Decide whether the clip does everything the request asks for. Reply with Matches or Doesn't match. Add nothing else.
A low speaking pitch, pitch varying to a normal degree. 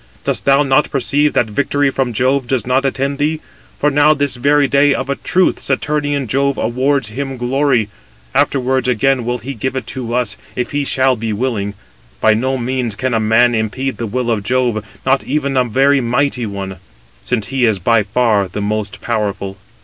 Matches